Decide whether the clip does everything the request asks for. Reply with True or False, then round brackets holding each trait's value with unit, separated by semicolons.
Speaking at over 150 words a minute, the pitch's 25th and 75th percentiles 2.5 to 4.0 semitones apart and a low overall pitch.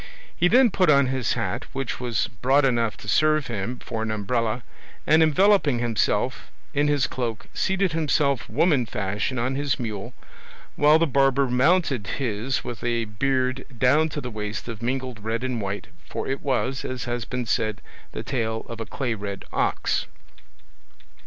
True (170 wpm; 3.6 semitones; 125 Hz)